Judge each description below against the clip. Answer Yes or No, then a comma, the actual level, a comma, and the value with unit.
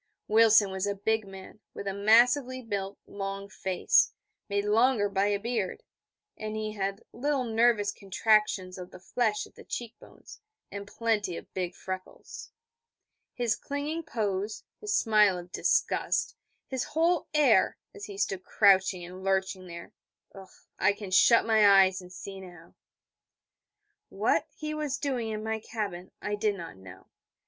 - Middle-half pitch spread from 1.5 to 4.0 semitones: Yes, average, 3.0 semitones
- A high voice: Yes, high, 205 Hz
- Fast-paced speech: No, average, 155 wpm